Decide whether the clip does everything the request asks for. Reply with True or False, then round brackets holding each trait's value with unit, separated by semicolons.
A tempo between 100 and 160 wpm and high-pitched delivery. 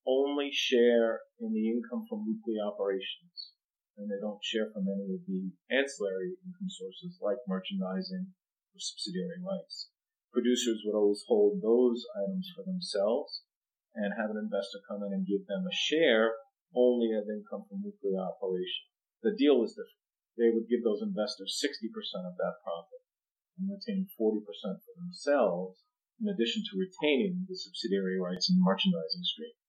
False (155 wpm; 135 Hz)